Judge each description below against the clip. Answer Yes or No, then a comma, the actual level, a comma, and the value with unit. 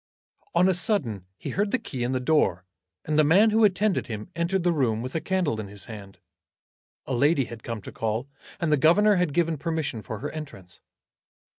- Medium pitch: Yes, medium, 150 Hz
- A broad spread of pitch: Yes, wide, 7.8 semitones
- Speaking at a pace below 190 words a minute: No, fast, 205 wpm